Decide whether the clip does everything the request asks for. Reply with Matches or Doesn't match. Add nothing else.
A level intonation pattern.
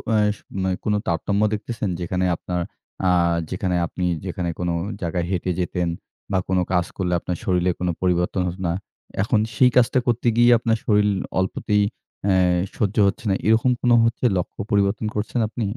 Doesn't match